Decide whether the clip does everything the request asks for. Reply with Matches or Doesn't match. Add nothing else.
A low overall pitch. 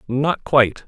Matches